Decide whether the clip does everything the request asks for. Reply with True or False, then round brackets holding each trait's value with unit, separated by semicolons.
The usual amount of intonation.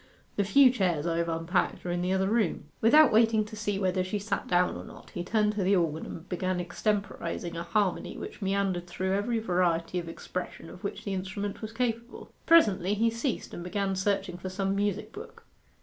True (3.0 semitones)